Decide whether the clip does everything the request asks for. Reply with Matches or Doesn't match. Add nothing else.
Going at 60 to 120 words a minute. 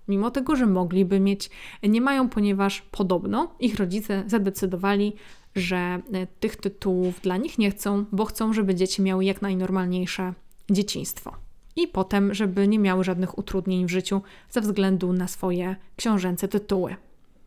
Doesn't match